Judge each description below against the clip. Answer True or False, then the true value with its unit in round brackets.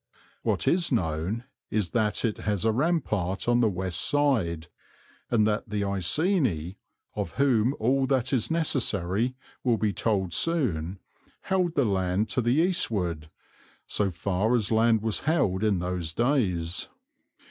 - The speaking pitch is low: True (110 Hz)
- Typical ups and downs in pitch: False (5.9 semitones)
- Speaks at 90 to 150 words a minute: True (145 wpm)